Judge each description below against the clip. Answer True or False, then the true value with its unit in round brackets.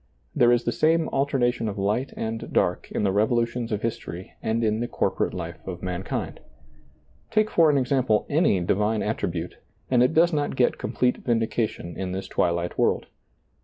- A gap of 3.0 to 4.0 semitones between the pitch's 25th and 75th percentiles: False (4.6 semitones)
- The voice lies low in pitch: True (115 Hz)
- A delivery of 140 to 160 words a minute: False (175 wpm)